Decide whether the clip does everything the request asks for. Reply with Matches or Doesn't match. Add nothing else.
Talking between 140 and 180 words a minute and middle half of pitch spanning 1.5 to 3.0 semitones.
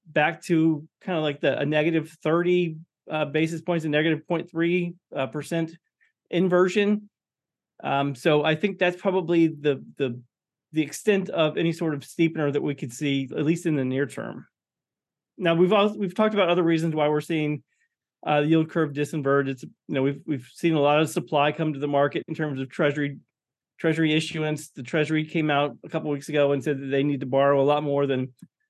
Doesn't match